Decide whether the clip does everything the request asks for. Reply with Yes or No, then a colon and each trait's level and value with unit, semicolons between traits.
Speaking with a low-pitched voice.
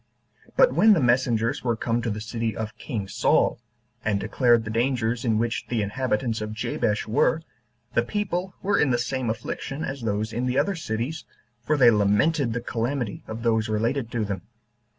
Yes: low, 115 Hz